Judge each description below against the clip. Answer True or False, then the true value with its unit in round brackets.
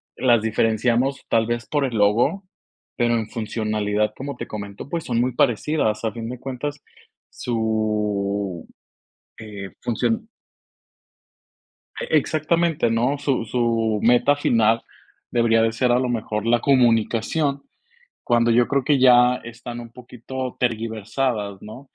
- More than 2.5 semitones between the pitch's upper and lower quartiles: True (2.9 semitones)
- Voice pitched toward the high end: False (120 Hz)